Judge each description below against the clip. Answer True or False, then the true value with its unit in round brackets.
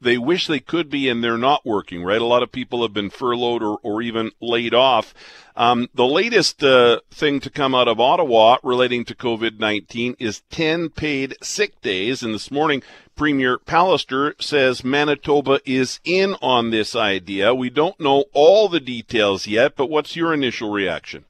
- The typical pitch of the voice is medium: False (125 Hz)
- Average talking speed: True (180 wpm)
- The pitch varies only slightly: False (3.8 semitones)